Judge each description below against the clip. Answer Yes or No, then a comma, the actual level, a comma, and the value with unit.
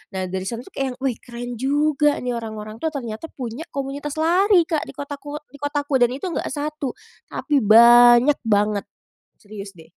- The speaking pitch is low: No, very high, 265 Hz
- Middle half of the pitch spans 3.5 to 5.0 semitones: Yes, average, 4.4 semitones